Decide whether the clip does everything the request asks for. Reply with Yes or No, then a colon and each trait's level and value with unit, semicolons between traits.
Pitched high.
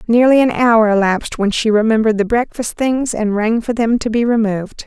Yes: high, 225 Hz